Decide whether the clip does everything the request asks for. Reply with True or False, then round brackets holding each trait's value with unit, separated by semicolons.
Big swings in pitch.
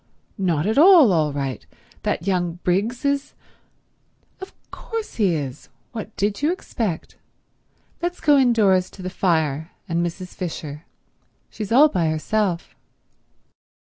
True (6.3 semitones)